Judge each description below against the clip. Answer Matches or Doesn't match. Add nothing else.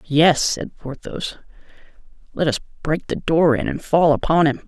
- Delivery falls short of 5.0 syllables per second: Matches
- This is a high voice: Doesn't match